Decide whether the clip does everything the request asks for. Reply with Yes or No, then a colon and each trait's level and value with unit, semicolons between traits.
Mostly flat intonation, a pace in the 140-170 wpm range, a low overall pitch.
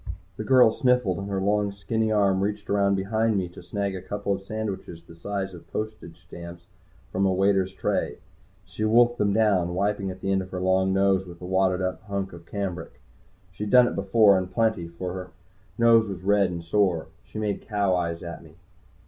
No: narrow, 2.2 semitones; average, 200 wpm; very low, 95 Hz